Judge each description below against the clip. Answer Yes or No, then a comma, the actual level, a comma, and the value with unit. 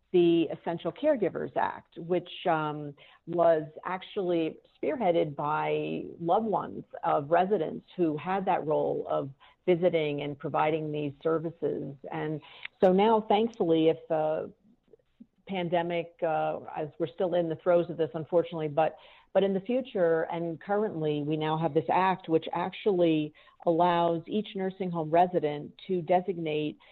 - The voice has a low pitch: No, medium, 170 Hz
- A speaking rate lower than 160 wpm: Yes, average, 140 wpm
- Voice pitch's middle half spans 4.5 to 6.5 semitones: No, average, 2.8 semitones